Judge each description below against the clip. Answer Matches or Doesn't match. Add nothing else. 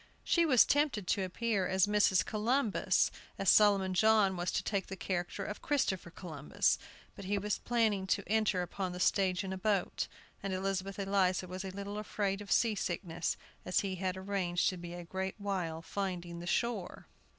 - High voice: Matches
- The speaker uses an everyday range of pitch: Doesn't match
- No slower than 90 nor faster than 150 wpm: Doesn't match